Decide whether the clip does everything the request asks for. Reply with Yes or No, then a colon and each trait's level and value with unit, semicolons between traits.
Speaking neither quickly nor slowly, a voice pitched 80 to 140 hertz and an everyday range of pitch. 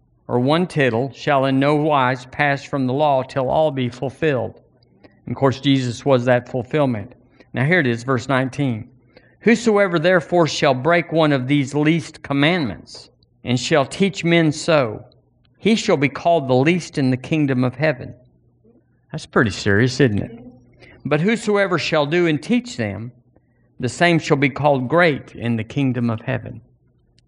Yes: average, 165 wpm; low, 135 Hz; average, 4.2 semitones